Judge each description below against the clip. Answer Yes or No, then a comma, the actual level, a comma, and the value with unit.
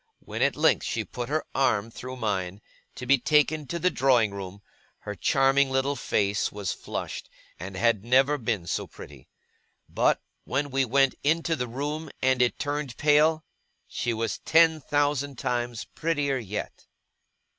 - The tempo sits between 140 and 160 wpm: Yes, average, 155 wpm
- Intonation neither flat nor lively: Yes, average, 4.6 semitones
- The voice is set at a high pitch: No, low, 130 Hz